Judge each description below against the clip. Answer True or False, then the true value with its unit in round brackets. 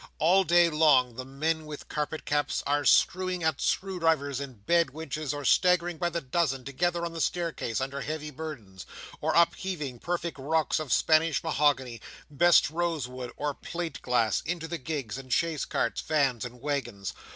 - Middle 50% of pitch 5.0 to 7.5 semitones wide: False (4.1 semitones)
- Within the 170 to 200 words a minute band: True (175 wpm)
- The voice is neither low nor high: True (150 Hz)